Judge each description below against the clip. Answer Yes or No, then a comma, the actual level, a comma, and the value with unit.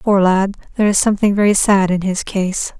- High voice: Yes, high, 195 Hz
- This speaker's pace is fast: Yes, fast, 215 wpm